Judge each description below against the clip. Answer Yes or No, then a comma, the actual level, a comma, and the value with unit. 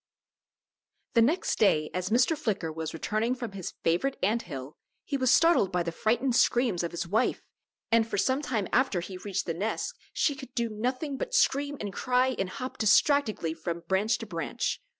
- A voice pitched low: No, high, 220 Hz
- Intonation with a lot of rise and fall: Yes, wide, 6.1 semitones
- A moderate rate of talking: Yes, average, 190 wpm